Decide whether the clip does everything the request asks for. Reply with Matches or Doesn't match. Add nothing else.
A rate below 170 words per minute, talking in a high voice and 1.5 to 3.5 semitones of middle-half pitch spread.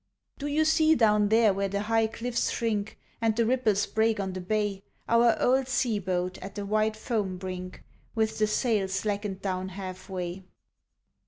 Doesn't match